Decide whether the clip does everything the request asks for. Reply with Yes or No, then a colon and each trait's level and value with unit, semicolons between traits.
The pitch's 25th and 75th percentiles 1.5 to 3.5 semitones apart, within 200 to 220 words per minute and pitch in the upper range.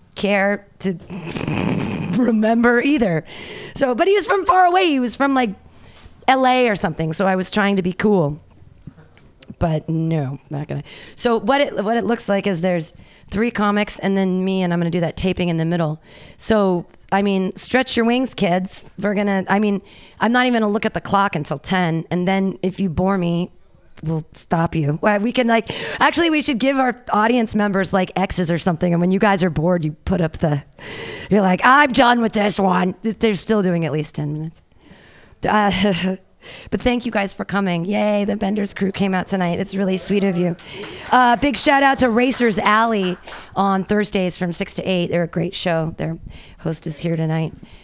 No: average, 4.0 semitones; fast, 205 wpm; high, 195 Hz